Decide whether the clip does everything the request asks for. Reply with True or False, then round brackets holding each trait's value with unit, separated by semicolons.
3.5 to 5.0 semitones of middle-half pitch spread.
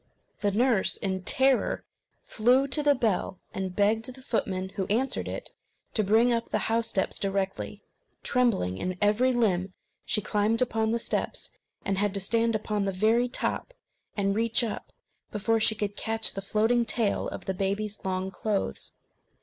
False (3.0 semitones)